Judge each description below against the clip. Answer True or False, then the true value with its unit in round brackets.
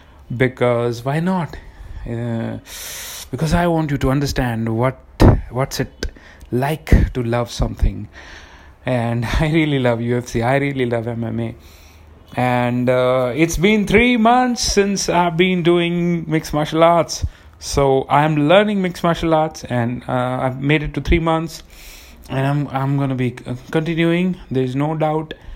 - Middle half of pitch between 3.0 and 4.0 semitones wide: False (5.6 semitones)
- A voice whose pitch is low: True (130 Hz)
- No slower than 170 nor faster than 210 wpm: False (150 wpm)